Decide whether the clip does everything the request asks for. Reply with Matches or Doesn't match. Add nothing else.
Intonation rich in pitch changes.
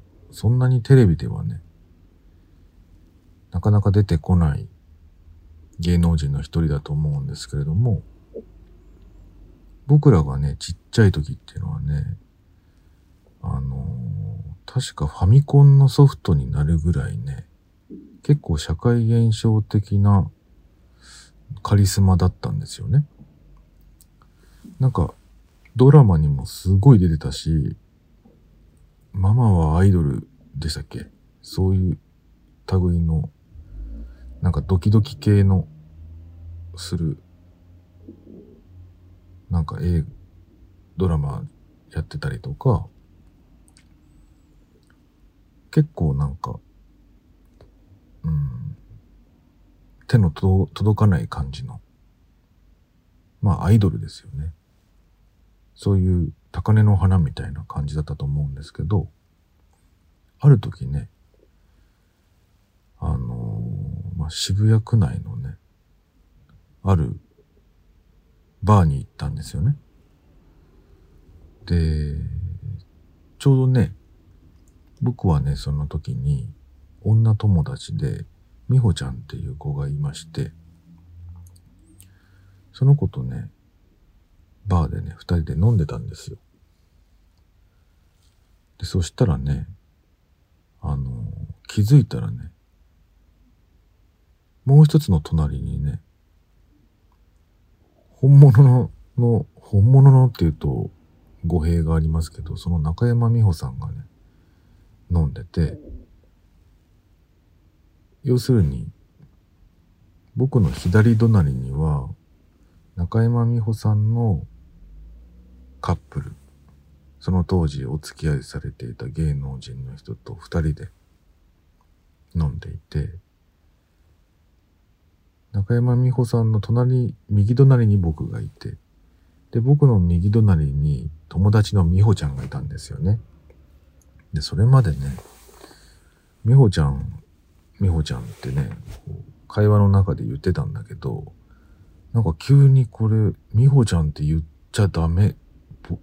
Doesn't match